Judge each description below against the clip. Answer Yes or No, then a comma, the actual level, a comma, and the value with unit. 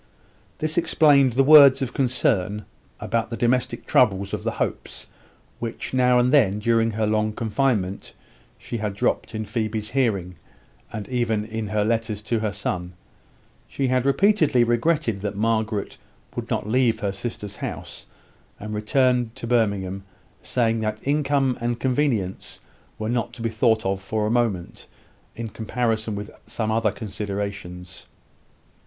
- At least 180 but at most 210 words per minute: No, average, 150 wpm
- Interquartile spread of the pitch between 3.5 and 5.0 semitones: No, average, 3.0 semitones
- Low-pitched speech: Yes, low, 115 Hz